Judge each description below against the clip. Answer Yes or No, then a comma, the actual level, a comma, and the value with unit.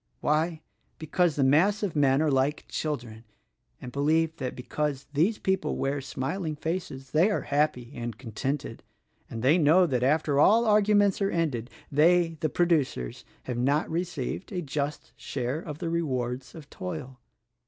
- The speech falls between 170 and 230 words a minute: No, average, 155 wpm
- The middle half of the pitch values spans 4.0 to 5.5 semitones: Yes, average, 4.3 semitones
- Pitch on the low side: No, medium, 150 Hz